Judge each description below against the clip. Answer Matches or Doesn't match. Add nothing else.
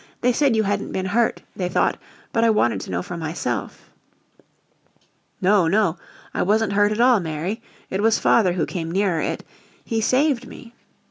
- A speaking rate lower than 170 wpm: Doesn't match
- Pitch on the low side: Doesn't match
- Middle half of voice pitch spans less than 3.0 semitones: Doesn't match